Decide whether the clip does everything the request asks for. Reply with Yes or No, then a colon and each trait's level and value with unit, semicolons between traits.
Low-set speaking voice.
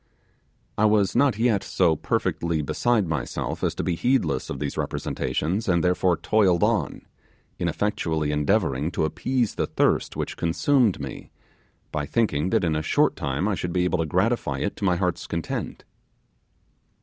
Yes: very low, 90 Hz